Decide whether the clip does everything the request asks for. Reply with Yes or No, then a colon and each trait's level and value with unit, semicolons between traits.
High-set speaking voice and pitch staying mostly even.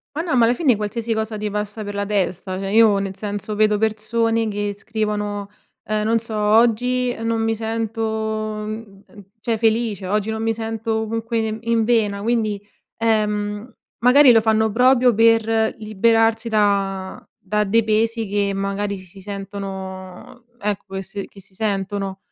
Yes: high, 215 Hz; narrow, 1.9 semitones